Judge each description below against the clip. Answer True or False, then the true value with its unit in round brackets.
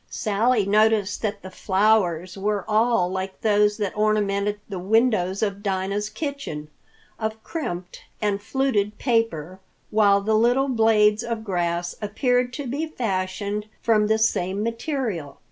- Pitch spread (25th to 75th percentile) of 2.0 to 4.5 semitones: True (2.7 semitones)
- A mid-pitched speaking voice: False (210 Hz)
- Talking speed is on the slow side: True (130 wpm)